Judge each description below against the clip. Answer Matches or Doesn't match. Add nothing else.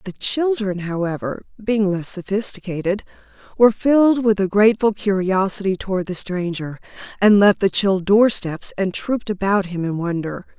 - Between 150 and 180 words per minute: Matches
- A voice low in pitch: Doesn't match